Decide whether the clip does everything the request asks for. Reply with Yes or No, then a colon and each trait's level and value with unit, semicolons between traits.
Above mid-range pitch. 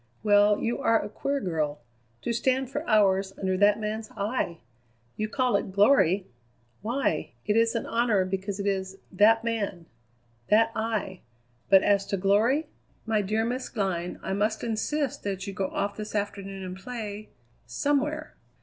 Yes: high, 210 Hz